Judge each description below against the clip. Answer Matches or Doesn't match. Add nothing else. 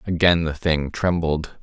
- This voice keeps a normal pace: Matches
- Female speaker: Doesn't match